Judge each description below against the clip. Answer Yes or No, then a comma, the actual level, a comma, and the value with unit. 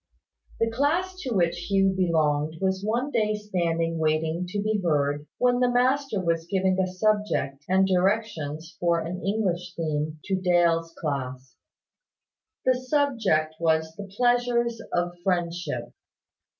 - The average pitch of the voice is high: No, medium, 180 Hz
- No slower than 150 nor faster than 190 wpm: No, slow, 135 wpm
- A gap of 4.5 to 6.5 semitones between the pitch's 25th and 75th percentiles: Yes, average, 4.9 semitones